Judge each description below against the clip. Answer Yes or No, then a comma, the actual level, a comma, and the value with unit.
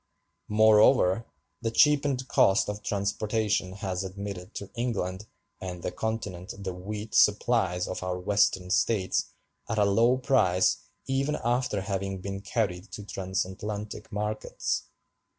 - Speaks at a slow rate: Yes, slow, 125 wpm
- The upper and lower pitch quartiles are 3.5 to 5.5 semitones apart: No, average, 2.9 semitones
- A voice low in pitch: Yes, low, 100 Hz